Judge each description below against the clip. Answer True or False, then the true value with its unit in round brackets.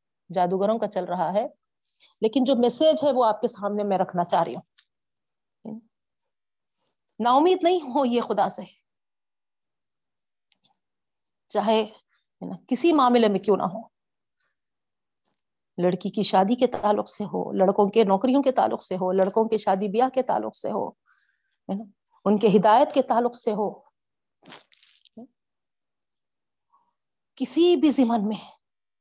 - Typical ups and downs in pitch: True (4.2 semitones)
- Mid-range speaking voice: False (220 Hz)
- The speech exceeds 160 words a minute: False (135 wpm)